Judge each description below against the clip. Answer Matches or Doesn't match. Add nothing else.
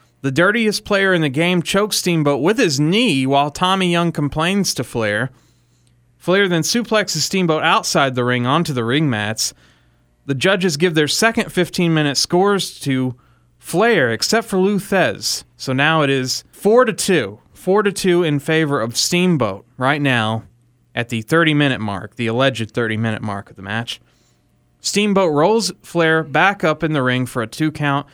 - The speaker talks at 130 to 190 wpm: Matches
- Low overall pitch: Doesn't match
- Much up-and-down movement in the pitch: Matches